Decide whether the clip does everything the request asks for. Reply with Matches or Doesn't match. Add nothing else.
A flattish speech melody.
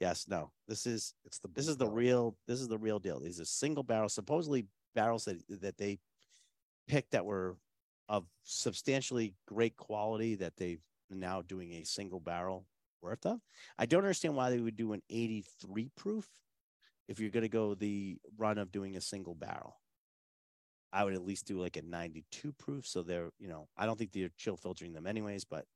Doesn't match